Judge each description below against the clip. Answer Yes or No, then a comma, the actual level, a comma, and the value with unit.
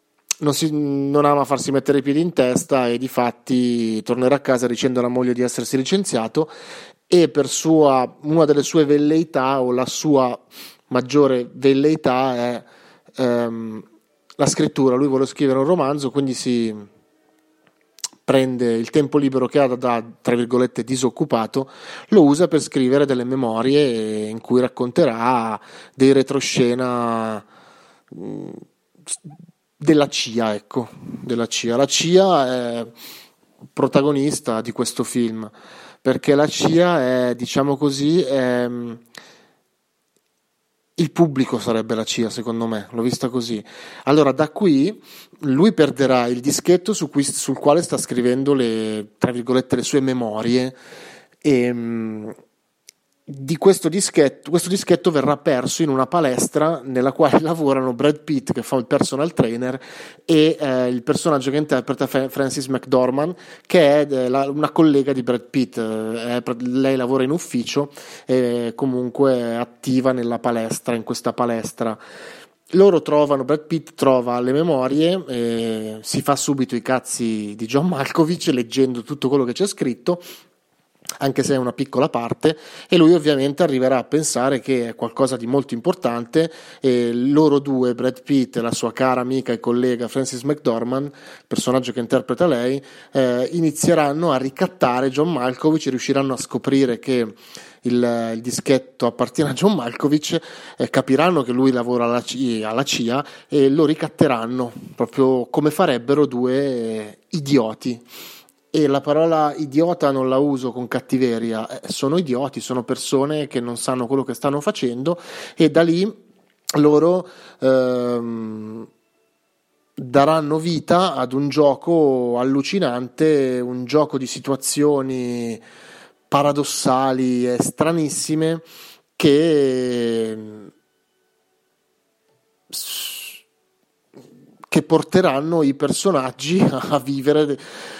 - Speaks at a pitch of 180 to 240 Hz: No, low, 135 Hz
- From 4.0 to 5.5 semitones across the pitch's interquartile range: No, average, 3.3 semitones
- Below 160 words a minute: Yes, average, 135 wpm